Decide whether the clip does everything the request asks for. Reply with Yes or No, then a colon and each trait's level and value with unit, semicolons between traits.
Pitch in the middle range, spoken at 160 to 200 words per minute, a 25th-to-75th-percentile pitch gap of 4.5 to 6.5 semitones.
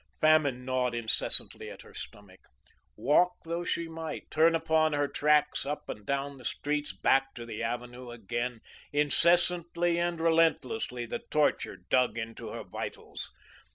No: medium, 145 Hz; average, 145 wpm; average, 4.9 semitones